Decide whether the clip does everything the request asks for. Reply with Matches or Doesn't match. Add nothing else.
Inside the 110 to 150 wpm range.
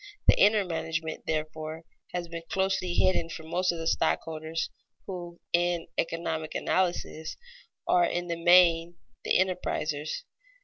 Matches